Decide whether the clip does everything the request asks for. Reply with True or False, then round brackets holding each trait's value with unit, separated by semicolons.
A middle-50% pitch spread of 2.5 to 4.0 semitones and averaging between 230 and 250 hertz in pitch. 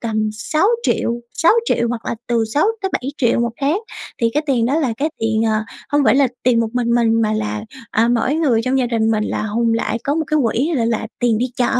True (3.7 semitones; 235 Hz)